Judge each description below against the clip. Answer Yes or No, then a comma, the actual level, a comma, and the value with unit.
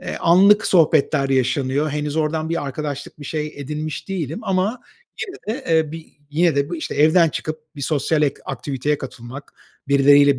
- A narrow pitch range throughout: Yes, narrow, 2.3 semitones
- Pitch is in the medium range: Yes, medium, 150 Hz